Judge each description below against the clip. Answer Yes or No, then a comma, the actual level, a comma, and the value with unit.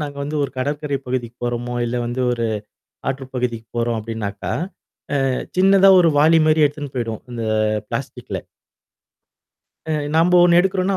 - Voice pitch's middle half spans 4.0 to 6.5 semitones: Yes, average, 5.0 semitones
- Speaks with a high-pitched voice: No, low, 135 Hz